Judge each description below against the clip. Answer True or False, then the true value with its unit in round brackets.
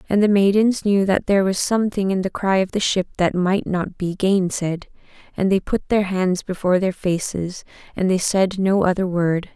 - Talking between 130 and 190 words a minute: False (205 wpm)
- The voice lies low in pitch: False (190 Hz)